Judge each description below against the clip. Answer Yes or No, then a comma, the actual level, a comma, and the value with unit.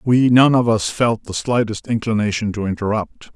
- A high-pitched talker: No, low, 110 Hz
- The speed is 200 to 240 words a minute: No, average, 180 wpm